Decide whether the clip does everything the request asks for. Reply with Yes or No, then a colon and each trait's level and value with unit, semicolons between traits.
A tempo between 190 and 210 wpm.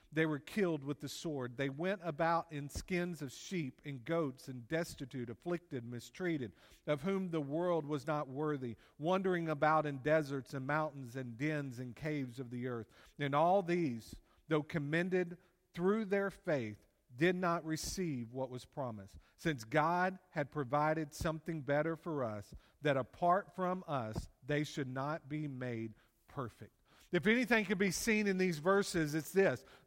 No: average, 165 wpm